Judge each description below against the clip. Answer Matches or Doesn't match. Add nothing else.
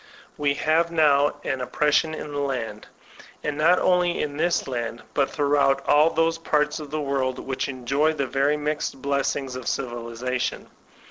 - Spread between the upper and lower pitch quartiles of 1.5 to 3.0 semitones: Matches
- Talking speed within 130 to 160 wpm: Doesn't match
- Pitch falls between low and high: Matches